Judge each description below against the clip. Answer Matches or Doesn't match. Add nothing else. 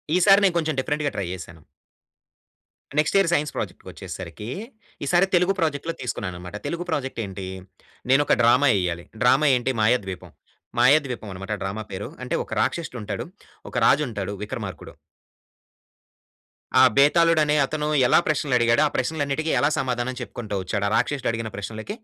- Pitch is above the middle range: Doesn't match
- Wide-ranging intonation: Matches